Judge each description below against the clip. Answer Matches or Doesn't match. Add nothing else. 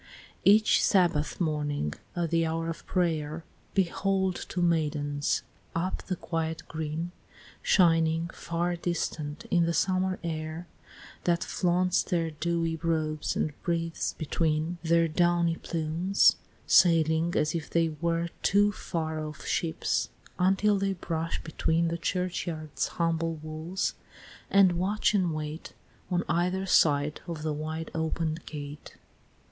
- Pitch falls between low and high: Matches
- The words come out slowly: Matches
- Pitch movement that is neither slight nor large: Doesn't match